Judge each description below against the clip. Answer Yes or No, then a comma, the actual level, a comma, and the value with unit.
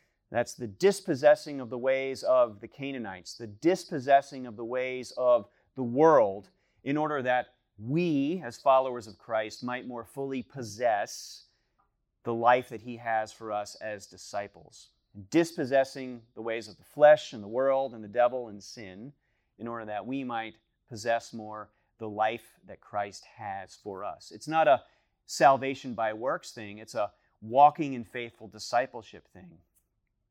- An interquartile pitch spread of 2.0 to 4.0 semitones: Yes, average, 3.7 semitones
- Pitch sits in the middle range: No, low, 120 Hz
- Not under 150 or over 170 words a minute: Yes, average, 160 wpm